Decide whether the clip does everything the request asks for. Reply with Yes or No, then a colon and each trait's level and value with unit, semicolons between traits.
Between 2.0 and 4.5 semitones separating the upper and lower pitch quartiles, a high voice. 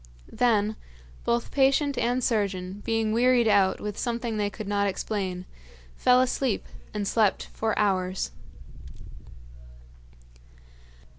Yes: average, 2.9 semitones; high, 215 Hz